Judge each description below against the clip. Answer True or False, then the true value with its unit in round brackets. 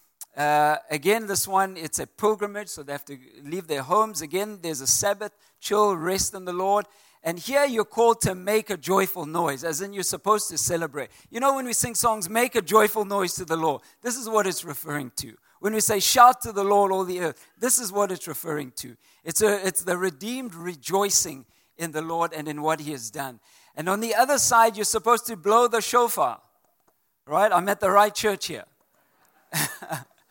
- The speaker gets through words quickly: True (210 wpm)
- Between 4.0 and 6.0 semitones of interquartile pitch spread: True (4.8 semitones)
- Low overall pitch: False (195 Hz)